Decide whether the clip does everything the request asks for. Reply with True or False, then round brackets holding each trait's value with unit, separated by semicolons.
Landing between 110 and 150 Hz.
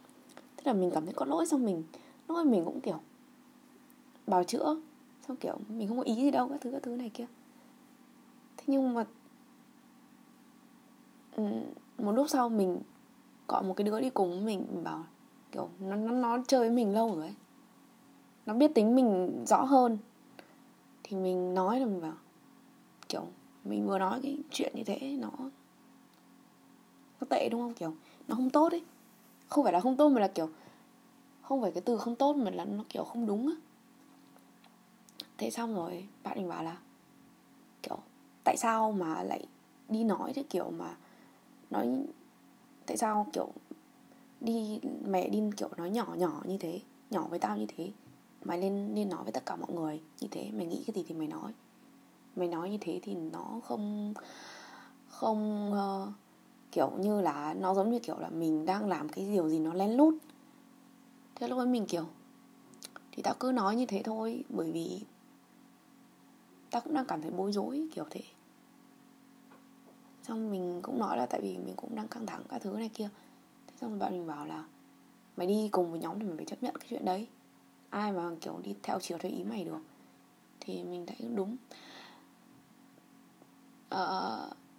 False (240 Hz)